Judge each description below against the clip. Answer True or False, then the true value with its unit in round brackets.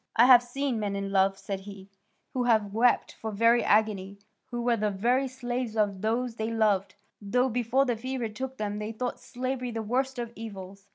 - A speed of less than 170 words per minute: False (195 wpm)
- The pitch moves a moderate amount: True (3.3 semitones)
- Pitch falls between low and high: False (225 Hz)